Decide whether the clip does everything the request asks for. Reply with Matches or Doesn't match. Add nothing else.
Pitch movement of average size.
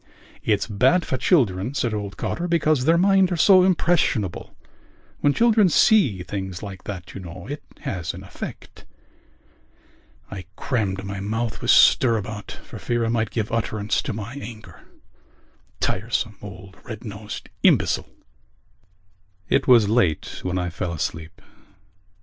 Doesn't match